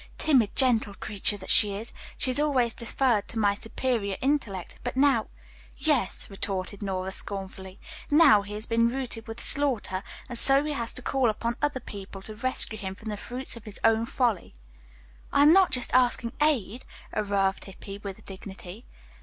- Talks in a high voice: Yes, high, 225 Hz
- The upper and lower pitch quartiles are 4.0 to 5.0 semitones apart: Yes, average, 4.4 semitones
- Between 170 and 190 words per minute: Yes, average, 175 wpm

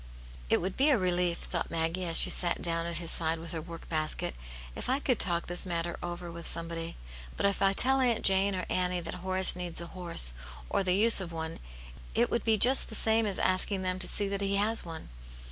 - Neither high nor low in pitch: Yes, medium, 180 Hz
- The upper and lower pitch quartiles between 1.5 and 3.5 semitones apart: Yes, average, 2.9 semitones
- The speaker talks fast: Yes, fast, 240 wpm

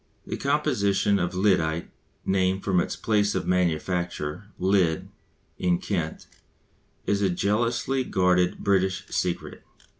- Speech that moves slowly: Yes, slow, 115 wpm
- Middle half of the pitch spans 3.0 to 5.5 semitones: No, narrow, 2.4 semitones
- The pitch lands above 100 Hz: No, very low, 95 Hz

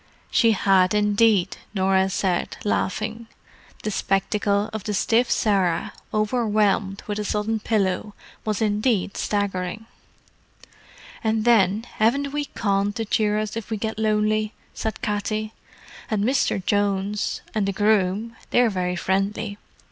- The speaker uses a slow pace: Yes, slow, 130 wpm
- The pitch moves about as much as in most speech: No, narrow, 1.9 semitones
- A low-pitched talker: No, high, 210 Hz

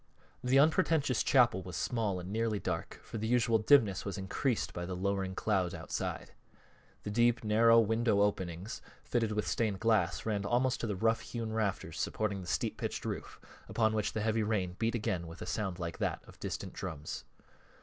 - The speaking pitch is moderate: No, low, 105 Hz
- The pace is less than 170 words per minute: No, average, 185 wpm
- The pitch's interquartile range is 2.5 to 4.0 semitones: Yes, average, 3.4 semitones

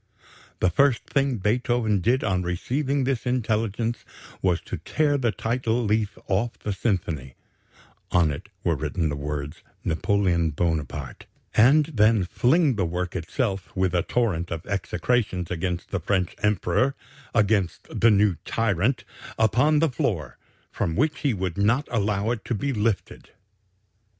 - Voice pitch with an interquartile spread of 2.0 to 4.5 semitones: No, wide, 5.4 semitones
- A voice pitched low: Yes, low, 105 Hz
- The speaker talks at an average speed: Yes, average, 145 wpm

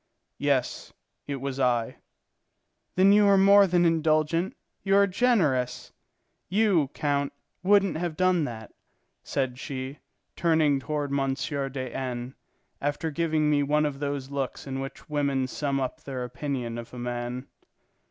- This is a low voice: No, medium, 145 Hz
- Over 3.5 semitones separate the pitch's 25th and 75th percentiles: Yes, average, 4.0 semitones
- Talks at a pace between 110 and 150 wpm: Yes, average, 140 wpm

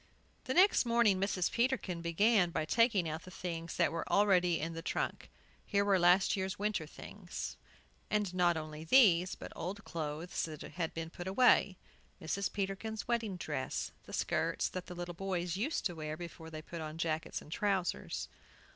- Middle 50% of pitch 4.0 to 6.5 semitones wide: No, average, 3.6 semitones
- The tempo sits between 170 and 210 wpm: Yes, average, 175 wpm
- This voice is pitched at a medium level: Yes, medium, 180 Hz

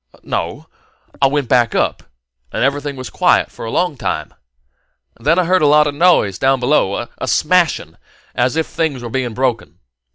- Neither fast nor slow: Yes, average, 180 wpm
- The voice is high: No, low, 135 Hz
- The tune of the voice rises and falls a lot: No, average, 3.9 semitones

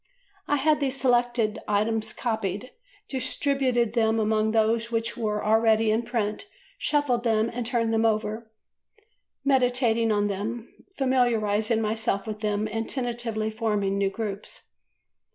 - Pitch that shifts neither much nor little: No, narrow, 2.0 semitones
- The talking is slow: Yes, slow, 130 wpm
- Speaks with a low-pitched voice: No, high, 225 Hz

